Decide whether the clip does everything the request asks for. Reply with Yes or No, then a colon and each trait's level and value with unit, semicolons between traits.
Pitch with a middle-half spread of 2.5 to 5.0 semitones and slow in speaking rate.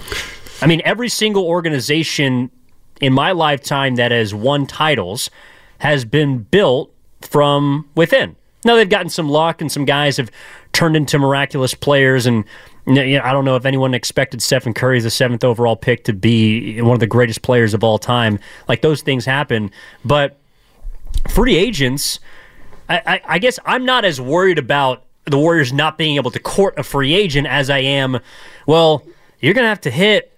No: average, 3.8 semitones; average, 180 wpm